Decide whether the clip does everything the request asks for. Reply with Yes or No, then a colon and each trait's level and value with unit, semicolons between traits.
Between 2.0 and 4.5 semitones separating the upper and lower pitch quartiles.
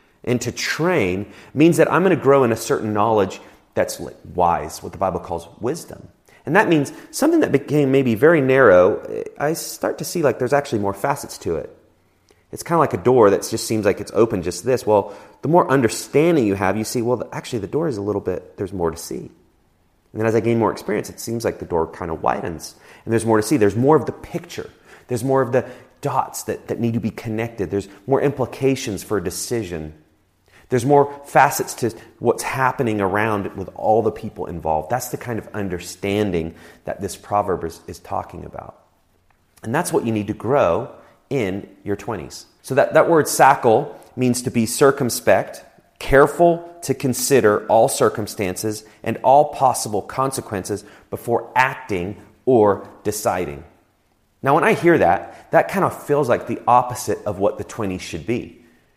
No: average, 5.2 semitones